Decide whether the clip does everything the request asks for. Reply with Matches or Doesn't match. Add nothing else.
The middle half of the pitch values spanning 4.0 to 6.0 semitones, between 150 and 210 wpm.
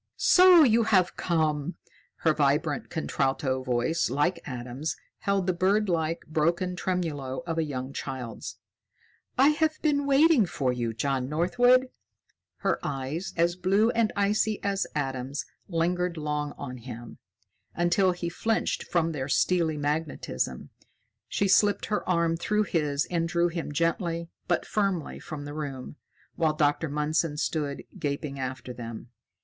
Doesn't match